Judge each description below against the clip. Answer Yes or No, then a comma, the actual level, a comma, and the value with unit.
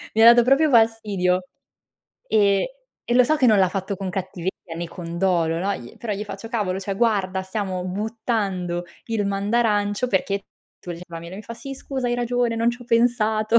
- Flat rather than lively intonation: No, average, 3.7 semitones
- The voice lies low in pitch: No, high, 205 Hz